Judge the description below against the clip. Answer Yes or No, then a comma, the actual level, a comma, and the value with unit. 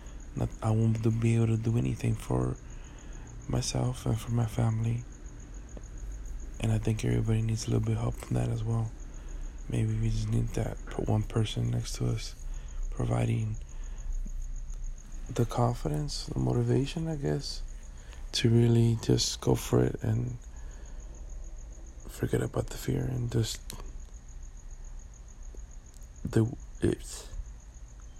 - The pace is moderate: No, slow, 125 wpm